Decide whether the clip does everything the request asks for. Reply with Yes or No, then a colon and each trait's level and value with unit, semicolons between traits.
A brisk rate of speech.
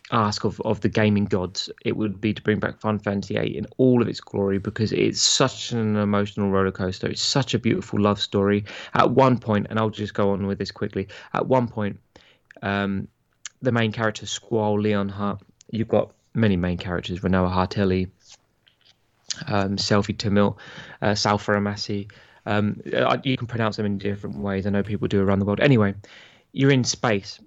No: average, 190 wpm